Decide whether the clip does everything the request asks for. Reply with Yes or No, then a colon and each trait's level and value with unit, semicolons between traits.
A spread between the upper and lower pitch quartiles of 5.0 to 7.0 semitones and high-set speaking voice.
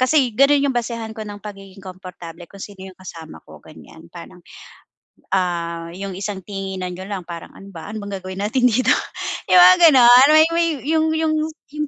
Yes: wide, 5.6 semitones; high, 205 Hz